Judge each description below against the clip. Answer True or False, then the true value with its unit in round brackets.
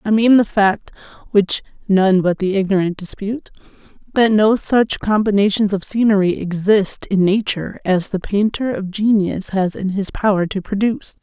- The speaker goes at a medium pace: True (160 wpm)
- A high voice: True (200 Hz)